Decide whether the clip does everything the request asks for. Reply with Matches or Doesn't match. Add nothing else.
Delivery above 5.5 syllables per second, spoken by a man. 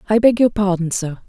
Doesn't match